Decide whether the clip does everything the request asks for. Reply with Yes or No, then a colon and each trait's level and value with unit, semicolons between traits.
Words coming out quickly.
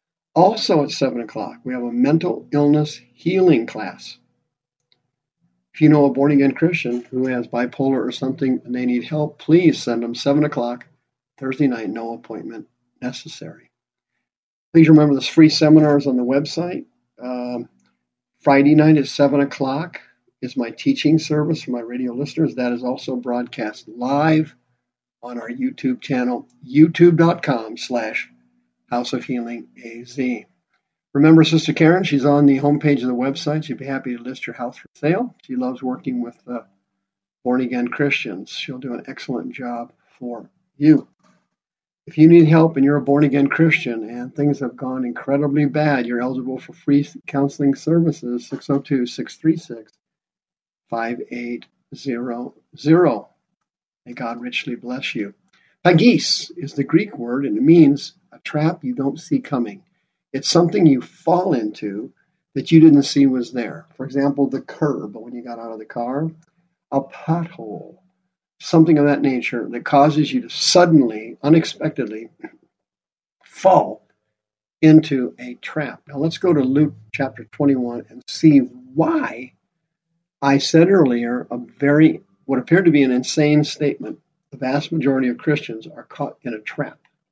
No: average, 150 wpm